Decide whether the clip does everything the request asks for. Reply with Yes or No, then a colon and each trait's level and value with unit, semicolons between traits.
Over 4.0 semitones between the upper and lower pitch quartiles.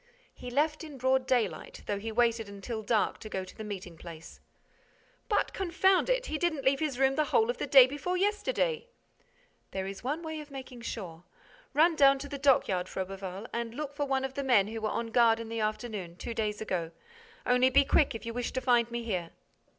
Yes: average, 5.2 semitones